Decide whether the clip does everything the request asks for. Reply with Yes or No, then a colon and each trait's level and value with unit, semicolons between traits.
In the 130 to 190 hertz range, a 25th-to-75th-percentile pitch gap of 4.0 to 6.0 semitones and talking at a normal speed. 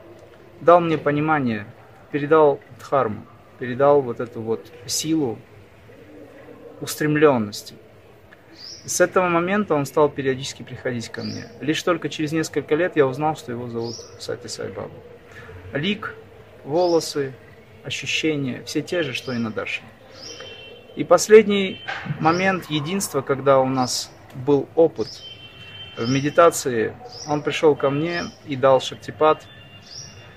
Yes: medium, 140 Hz; average, 5.0 semitones; average, 120 wpm